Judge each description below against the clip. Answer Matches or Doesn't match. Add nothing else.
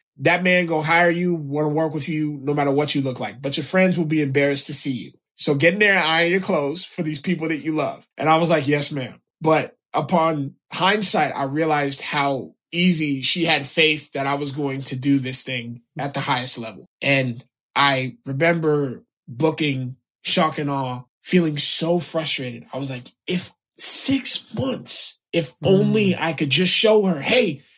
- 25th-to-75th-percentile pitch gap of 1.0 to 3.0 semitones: Doesn't match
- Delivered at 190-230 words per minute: Matches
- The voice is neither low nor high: Matches